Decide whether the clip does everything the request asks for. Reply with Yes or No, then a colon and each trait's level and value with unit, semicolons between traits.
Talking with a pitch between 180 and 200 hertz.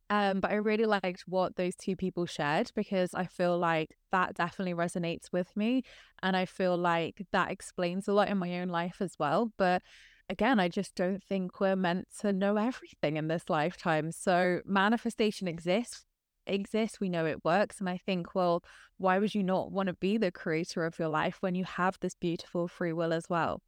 Yes: medium, 185 Hz